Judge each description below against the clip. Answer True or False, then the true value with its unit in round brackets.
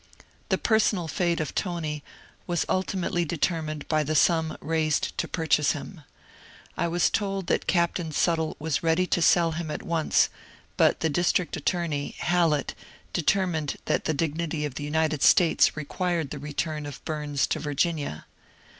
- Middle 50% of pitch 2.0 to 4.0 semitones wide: True (2.4 semitones)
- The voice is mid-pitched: True (160 Hz)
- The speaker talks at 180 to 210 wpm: False (155 wpm)